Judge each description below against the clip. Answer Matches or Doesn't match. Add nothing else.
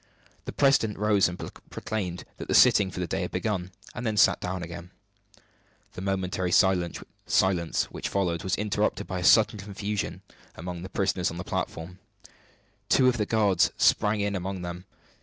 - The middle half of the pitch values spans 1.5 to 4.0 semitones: Matches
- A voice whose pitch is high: Doesn't match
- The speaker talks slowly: Doesn't match